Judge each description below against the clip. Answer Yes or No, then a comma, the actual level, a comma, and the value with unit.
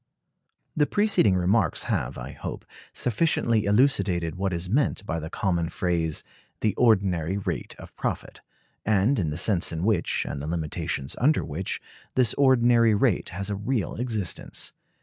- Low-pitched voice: Yes, low, 100 Hz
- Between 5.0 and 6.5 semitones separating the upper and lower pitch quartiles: Yes, average, 5.3 semitones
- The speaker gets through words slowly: No, average, 150 wpm